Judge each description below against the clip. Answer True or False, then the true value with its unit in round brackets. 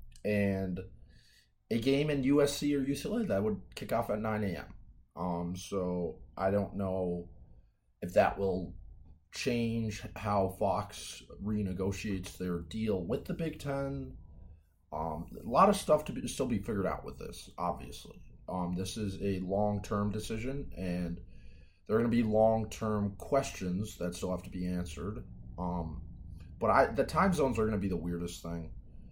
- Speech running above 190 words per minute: False (165 wpm)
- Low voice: True (95 Hz)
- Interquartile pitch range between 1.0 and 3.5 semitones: False (4.1 semitones)